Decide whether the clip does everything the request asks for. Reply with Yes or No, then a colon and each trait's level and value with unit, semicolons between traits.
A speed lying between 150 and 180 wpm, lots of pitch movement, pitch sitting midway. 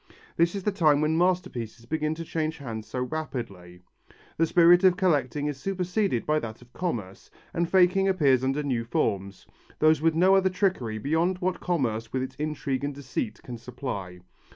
Yes: average, 175 wpm; wide, 6.3 semitones; medium, 150 Hz